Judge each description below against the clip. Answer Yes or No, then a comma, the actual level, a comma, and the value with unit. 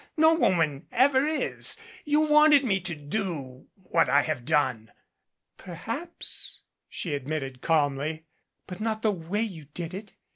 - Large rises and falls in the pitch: Yes, wide, 7.6 semitones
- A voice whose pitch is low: No, medium, 175 Hz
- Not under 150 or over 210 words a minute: No, average, 140 wpm